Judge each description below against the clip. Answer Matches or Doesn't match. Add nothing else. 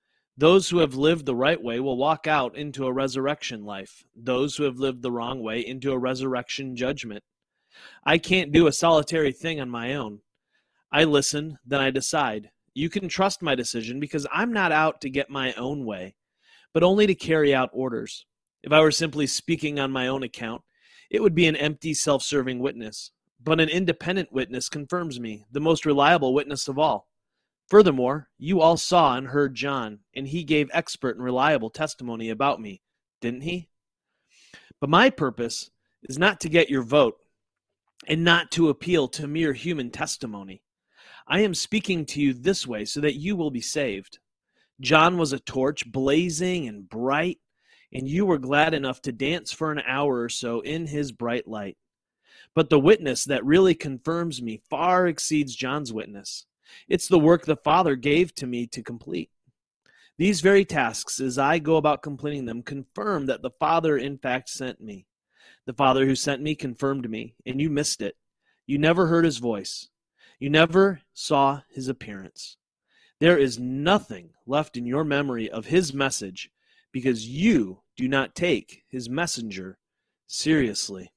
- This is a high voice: Doesn't match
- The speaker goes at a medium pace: Matches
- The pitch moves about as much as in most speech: Matches